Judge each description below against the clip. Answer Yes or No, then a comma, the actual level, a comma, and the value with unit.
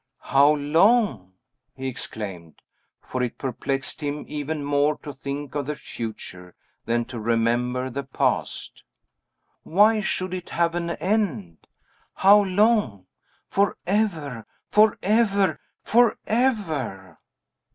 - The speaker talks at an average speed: No, slow, 105 wpm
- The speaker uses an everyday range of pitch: No, wide, 8.3 semitones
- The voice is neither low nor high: Yes, medium, 145 Hz